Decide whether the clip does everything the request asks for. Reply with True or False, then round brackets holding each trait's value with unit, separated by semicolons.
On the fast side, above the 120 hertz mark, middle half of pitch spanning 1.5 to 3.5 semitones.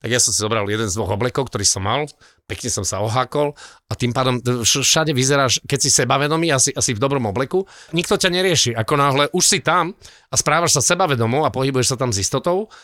False (220 wpm; 135 Hz; 4.3 semitones)